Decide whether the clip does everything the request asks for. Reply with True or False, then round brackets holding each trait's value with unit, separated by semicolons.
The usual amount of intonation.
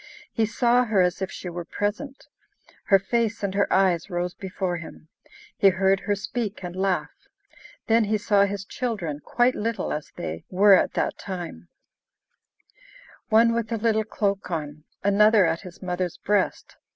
True (3.3 semitones)